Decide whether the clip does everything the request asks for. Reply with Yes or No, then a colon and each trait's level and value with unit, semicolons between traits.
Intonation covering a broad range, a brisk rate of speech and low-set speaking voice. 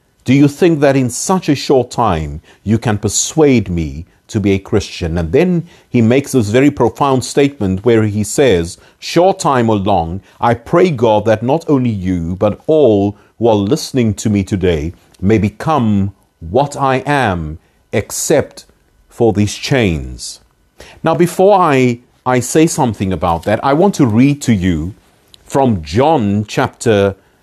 No: wide, 6.0 semitones; average, 160 wpm; low, 115 Hz